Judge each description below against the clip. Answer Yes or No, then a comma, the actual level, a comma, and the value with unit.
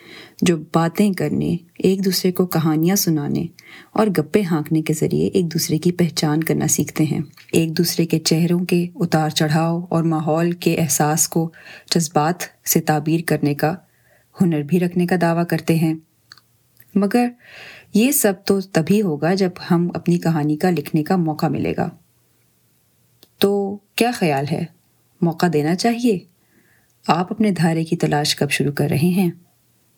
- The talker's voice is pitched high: No, medium, 170 Hz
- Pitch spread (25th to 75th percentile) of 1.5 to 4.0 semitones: Yes, average, 2.9 semitones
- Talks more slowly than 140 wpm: No, average, 155 wpm